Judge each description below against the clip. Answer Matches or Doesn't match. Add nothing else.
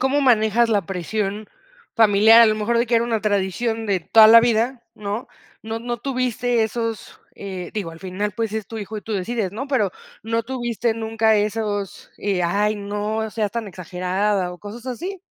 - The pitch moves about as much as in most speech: Doesn't match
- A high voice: Matches